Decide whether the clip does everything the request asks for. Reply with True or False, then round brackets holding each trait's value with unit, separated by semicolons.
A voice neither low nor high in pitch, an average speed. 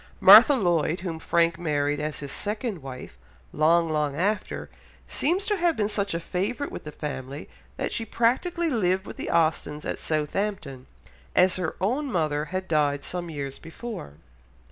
True (170 Hz; 165 wpm)